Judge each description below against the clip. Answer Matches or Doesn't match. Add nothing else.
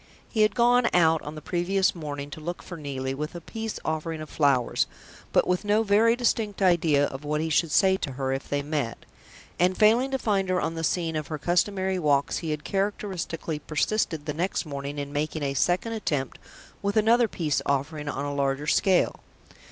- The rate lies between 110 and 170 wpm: Doesn't match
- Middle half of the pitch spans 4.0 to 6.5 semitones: Matches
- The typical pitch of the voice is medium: Matches